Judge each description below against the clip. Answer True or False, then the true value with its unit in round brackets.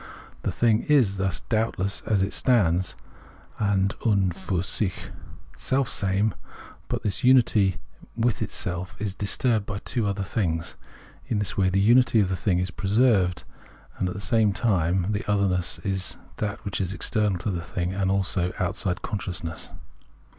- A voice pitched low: True (100 Hz)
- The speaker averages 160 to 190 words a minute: False (150 wpm)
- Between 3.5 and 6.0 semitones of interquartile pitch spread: False (2.7 semitones)